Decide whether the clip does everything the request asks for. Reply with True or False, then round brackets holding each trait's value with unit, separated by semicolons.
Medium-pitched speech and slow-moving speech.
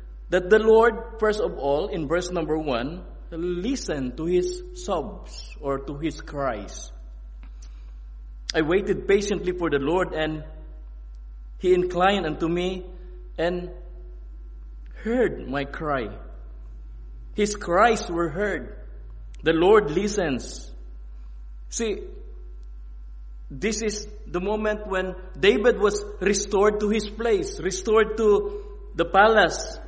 True (175 Hz; 110 wpm)